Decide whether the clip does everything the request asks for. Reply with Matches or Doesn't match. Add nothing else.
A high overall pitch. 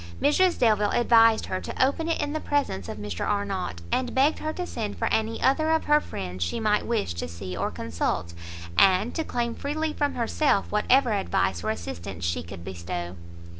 Matches